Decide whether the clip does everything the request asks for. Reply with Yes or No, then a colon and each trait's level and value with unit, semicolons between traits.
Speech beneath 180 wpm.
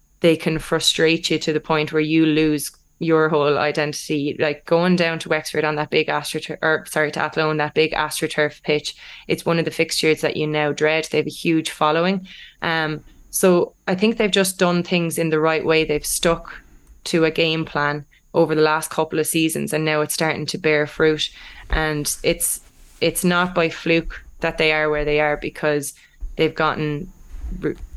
No: average, 195 wpm